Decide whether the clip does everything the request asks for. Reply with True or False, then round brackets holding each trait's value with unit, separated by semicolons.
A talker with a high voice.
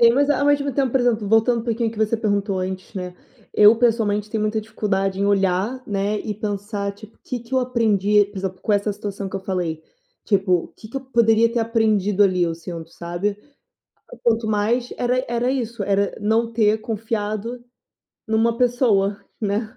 True (215 Hz)